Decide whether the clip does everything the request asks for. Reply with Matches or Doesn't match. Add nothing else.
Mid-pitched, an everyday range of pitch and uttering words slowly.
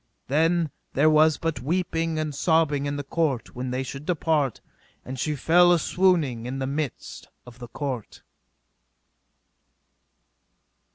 Matches